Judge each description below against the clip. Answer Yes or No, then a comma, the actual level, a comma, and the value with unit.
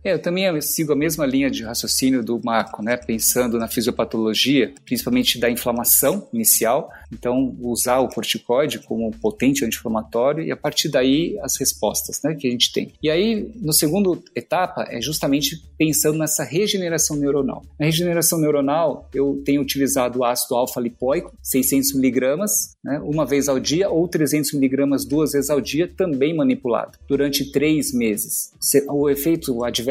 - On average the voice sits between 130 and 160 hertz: Yes, medium, 140 Hz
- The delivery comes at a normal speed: Yes, average, 155 wpm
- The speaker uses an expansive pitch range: No, average, 4.3 semitones